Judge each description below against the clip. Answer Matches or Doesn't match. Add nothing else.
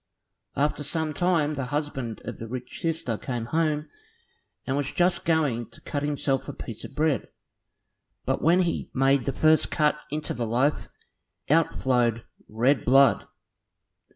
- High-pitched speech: Doesn't match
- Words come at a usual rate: Matches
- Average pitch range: Matches